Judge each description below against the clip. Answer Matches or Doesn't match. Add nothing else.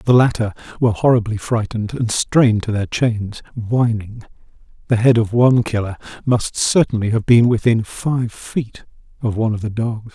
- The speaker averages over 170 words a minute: Doesn't match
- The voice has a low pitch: Matches